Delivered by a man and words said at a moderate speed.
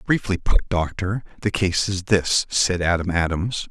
Yes: male; average, 160 wpm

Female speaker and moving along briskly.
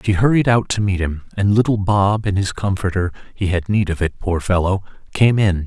No: male; fast, 210 wpm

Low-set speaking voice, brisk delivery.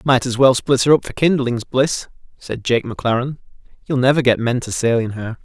Yes: low, 125 Hz; fast, 220 wpm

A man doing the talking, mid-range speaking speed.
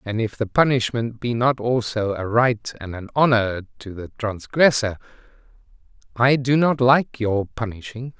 Yes: male; average, 155 wpm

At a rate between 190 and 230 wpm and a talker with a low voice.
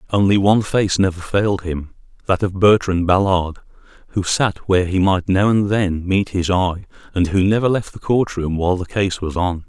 Yes: fast, 205 wpm; very low, 95 Hz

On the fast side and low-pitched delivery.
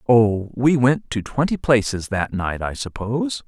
No: average, 175 wpm; low, 120 Hz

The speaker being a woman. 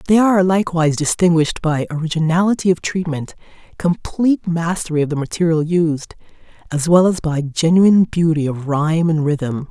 Yes: female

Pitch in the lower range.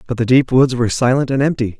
Yes: low, 125 Hz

